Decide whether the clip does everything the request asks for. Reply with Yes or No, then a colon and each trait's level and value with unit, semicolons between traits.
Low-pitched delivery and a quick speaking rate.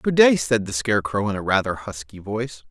Yes: low, 110 Hz; fast, 220 wpm